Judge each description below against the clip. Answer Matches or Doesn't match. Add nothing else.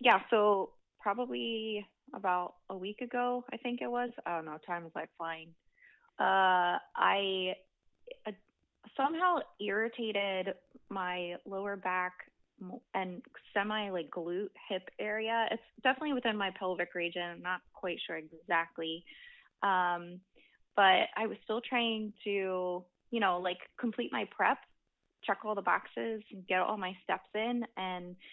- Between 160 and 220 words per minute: Doesn't match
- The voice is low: Doesn't match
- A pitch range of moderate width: Matches